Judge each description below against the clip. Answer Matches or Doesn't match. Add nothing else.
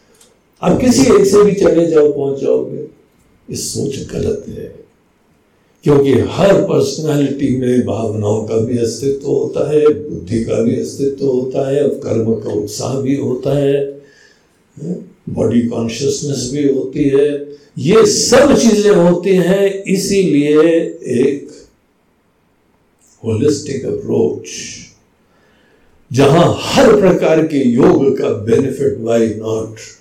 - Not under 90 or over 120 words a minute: Matches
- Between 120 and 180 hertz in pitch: Matches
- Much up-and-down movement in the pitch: Matches